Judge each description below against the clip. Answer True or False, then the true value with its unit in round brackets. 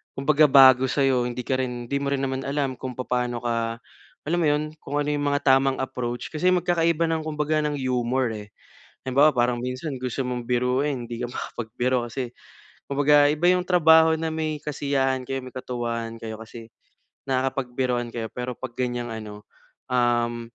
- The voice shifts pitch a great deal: False (3.0 semitones)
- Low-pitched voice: True (130 Hz)